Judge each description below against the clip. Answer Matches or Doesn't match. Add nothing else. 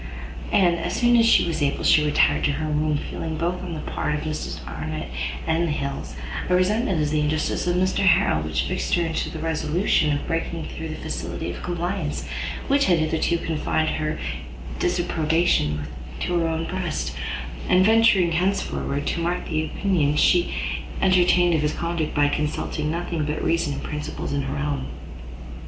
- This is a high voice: Doesn't match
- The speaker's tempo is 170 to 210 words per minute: Matches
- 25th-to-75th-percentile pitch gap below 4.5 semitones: Matches